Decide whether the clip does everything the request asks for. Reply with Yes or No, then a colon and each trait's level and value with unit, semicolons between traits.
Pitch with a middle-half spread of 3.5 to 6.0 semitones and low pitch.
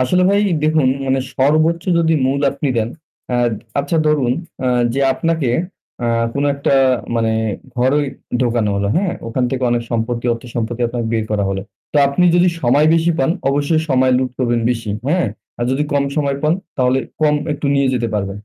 Yes: average, 4.0 semitones; low, 130 Hz